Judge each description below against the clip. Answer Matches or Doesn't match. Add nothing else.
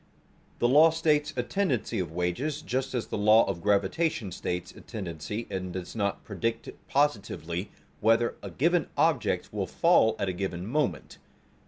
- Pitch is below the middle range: Matches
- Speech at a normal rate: Matches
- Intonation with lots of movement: Matches